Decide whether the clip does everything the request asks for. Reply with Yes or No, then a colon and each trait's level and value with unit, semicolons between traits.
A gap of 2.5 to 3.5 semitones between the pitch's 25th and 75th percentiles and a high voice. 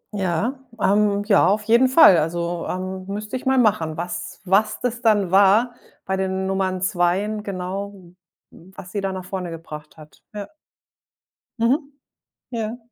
Yes: average, 2.9 semitones; high, 195 Hz